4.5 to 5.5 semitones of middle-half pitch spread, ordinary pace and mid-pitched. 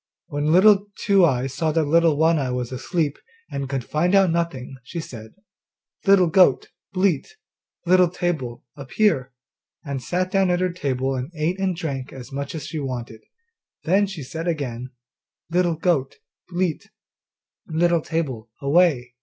Yes: average, 5.0 semitones; average, 155 wpm; medium, 160 Hz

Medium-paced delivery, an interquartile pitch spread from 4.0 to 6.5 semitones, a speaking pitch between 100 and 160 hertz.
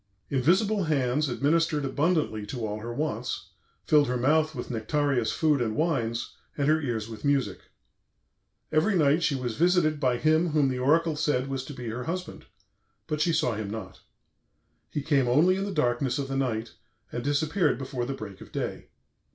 Yes: average, 180 wpm; average, 4.3 semitones; medium, 140 Hz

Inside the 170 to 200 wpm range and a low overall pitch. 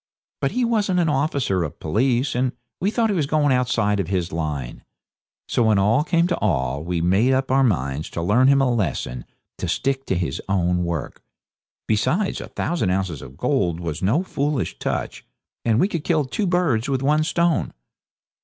Yes: average, 190 wpm; low, 120 Hz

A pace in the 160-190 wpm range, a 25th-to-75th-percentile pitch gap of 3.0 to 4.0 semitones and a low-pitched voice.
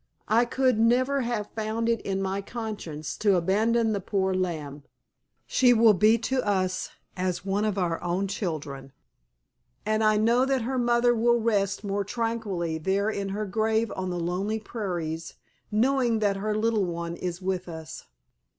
No: average, 165 wpm; average, 3.7 semitones; high, 205 Hz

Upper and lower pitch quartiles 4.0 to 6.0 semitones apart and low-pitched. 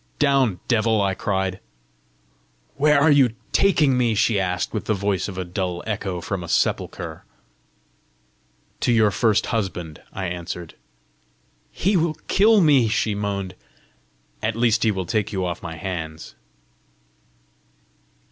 Yes: average, 4.6 semitones; low, 105 Hz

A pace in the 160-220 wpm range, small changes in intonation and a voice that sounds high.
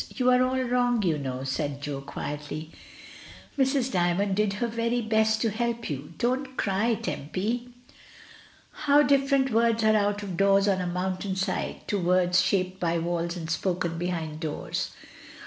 No: average, 165 wpm; wide, 5.4 semitones; high, 195 Hz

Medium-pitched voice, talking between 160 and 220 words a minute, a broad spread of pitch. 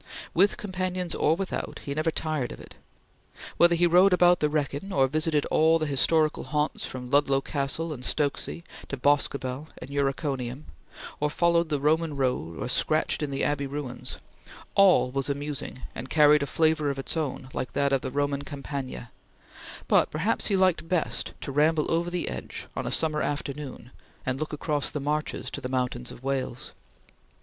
No: medium, 145 Hz; average, 175 wpm; average, 2.9 semitones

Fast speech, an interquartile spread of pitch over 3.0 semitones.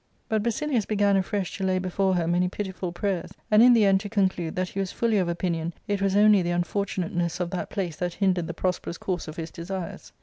No: fast, 230 wpm; narrow, 2.5 semitones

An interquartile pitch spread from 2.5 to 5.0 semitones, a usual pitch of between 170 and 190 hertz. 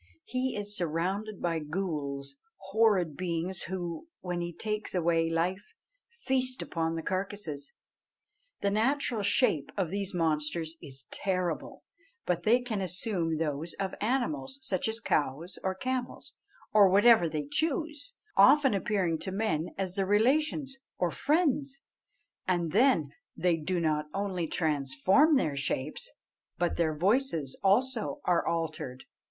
No: wide, 5.5 semitones; medium, 185 Hz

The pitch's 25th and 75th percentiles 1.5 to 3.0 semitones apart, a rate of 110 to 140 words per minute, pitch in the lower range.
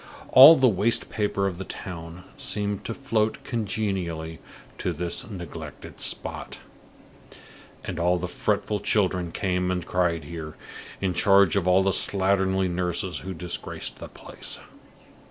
Yes: narrow, 2.6 semitones; slow, 135 wpm; very low, 95 Hz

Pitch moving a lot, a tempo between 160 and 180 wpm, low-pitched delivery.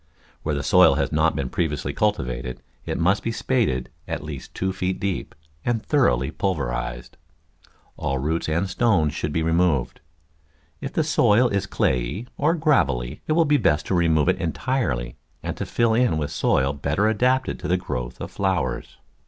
Yes: wide, 7.8 semitones; average, 170 wpm; very low, 80 Hz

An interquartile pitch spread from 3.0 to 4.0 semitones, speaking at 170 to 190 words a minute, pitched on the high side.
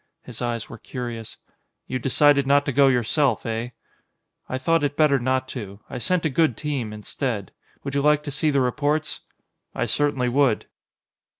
No: average, 3.3 semitones; average, 175 wpm; low, 135 Hz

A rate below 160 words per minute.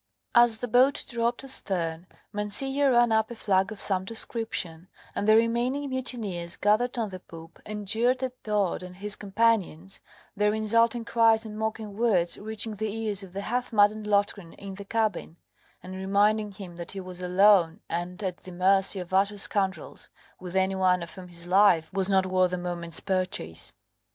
No: average, 180 wpm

